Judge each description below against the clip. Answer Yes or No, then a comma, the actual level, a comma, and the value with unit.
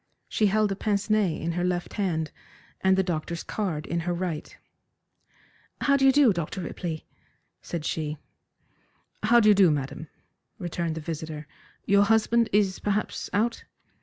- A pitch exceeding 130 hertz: Yes, medium, 185 Hz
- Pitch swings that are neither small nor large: Yes, average, 4.5 semitones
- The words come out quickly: No, average, 160 wpm